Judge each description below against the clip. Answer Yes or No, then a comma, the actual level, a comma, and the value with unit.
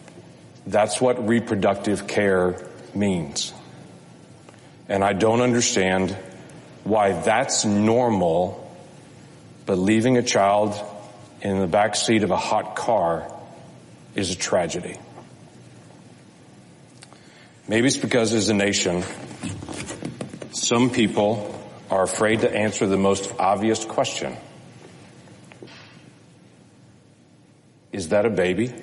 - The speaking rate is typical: No, slow, 100 wpm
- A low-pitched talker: Yes, low, 105 Hz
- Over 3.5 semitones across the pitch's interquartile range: No, narrow, 2.6 semitones